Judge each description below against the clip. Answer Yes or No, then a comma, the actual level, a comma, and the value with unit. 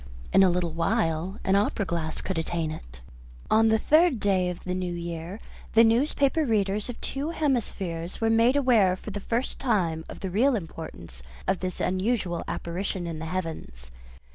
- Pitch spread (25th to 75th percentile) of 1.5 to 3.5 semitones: No, average, 5.1 semitones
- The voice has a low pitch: No, high, 190 Hz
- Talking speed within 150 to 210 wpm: Yes, average, 175 wpm